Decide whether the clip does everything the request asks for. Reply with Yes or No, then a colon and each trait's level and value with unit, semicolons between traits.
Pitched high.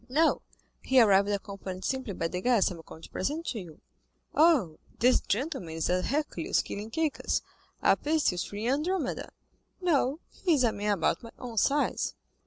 Yes: high, 235 Hz